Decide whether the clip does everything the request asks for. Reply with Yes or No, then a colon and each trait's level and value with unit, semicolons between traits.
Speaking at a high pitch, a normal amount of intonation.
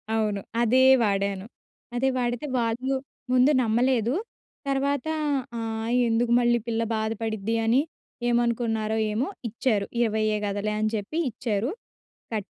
No: high, 225 Hz; narrow, 2.1 semitones